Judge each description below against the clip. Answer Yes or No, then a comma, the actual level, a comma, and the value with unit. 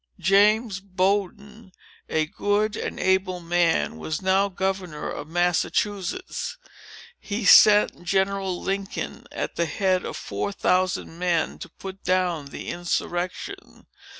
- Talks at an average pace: No, slow, 120 wpm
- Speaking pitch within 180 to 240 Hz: Yes, high, 190 Hz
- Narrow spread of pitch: Yes, narrow, 2.3 semitones